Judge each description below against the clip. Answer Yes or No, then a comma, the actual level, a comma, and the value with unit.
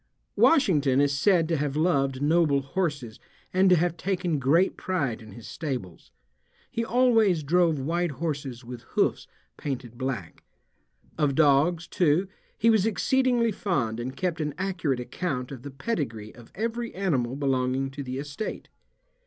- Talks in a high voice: No, medium, 150 Hz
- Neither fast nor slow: Yes, average, 150 wpm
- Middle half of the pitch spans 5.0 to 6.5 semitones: Yes, wide, 5.4 semitones